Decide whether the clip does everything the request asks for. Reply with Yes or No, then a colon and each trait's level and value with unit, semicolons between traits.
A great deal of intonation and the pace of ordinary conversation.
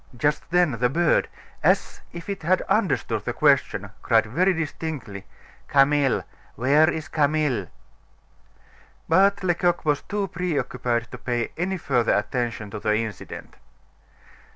No: wide, 6.2 semitones; slow, 130 wpm